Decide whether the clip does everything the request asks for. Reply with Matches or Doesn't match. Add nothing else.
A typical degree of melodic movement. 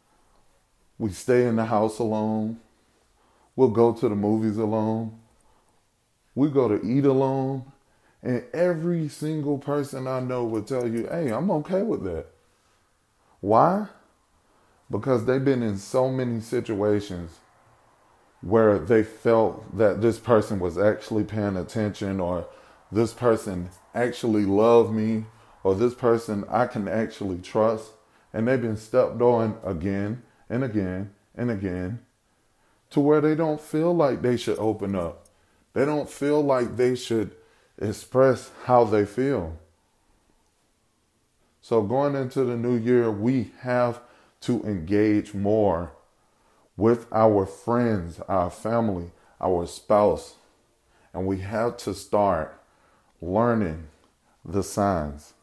Matches